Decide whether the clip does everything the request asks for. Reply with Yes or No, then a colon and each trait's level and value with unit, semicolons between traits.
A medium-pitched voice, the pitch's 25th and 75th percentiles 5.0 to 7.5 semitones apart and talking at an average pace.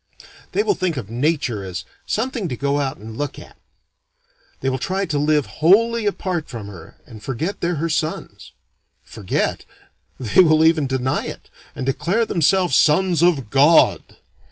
Yes: medium, 155 Hz; average, 5.3 semitones; average, 160 wpm